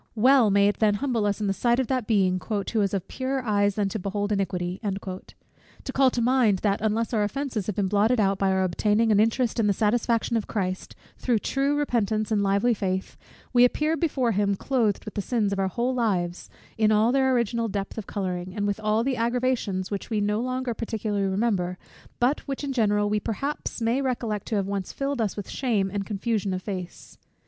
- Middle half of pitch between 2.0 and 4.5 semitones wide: Yes, average, 3.4 semitones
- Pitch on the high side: Yes, high, 215 Hz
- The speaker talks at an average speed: No, fast, 215 wpm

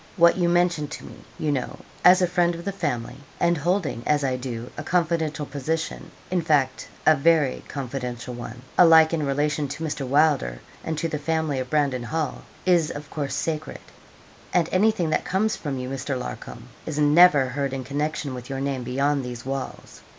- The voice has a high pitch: No, medium, 150 Hz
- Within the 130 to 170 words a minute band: No, average, 185 wpm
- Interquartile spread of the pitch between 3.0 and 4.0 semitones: Yes, average, 3.6 semitones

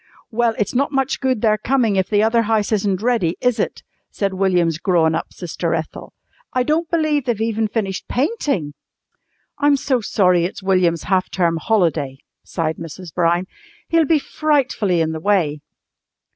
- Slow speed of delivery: No, average, 165 wpm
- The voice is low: No, high, 205 Hz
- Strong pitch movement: Yes, wide, 6.1 semitones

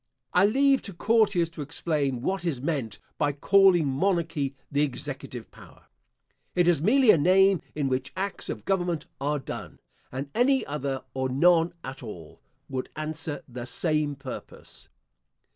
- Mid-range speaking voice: Yes, medium, 155 Hz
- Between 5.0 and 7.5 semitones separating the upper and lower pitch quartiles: Yes, wide, 5.4 semitones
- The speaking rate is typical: Yes, average, 150 wpm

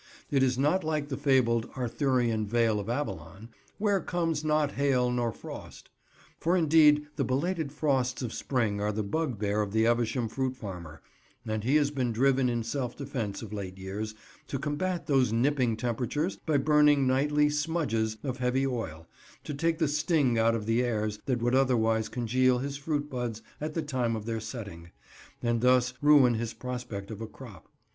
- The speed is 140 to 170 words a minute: No, average, 180 wpm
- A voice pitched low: Yes, low, 125 Hz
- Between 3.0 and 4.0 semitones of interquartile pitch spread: No, average, 4.4 semitones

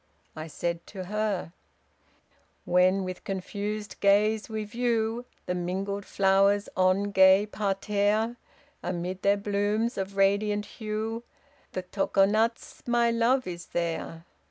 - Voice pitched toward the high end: Yes, high, 200 Hz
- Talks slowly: Yes, slow, 115 wpm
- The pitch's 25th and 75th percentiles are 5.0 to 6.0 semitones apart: No, narrow, 2.4 semitones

